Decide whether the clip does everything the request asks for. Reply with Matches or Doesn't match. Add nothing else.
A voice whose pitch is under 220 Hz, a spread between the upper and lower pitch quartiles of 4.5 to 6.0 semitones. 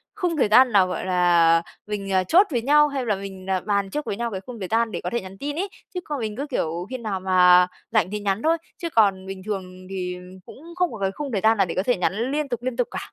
Matches